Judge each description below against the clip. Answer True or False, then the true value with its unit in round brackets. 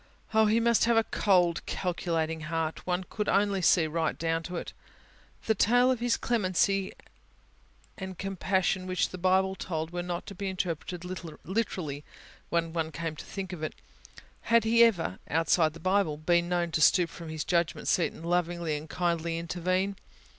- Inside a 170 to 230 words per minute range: True (175 wpm)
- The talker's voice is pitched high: False (180 Hz)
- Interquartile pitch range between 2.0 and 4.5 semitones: True (2.9 semitones)